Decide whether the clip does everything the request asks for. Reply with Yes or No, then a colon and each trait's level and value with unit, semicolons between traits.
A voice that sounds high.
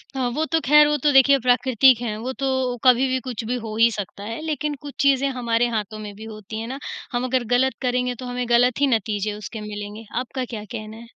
Yes: high, 245 Hz